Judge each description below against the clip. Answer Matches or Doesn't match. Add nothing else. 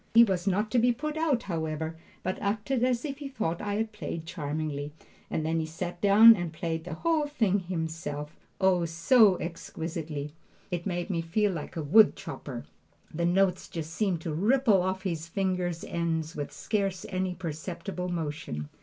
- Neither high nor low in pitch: Matches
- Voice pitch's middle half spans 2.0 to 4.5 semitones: Matches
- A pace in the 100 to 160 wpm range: Doesn't match